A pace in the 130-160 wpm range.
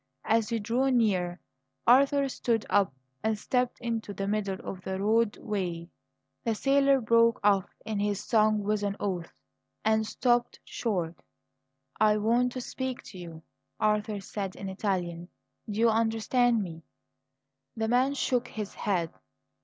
Yes: average, 145 wpm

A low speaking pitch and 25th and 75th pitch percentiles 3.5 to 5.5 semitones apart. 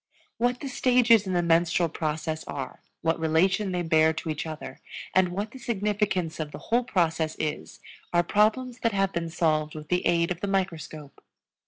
No: medium, 175 Hz; average, 4.5 semitones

